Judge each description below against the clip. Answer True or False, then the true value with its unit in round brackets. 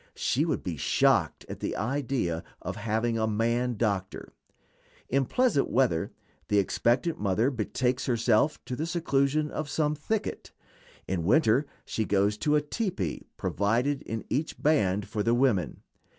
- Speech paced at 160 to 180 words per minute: False (150 wpm)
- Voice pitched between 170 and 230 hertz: False (120 Hz)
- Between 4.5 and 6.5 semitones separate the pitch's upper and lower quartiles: True (5.6 semitones)